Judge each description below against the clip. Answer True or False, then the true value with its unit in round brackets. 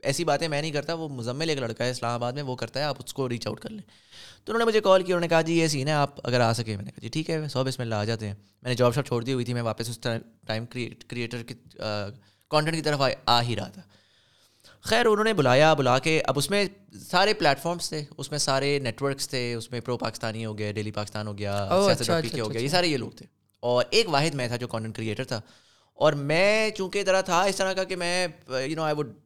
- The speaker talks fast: True (270 wpm)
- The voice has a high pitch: False (135 Hz)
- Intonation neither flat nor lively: False (5.7 semitones)